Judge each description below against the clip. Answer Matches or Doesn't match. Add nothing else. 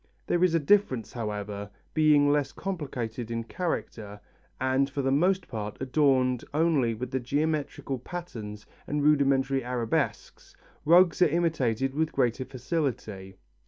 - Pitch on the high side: Doesn't match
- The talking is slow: Matches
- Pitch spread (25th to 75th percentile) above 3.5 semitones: Matches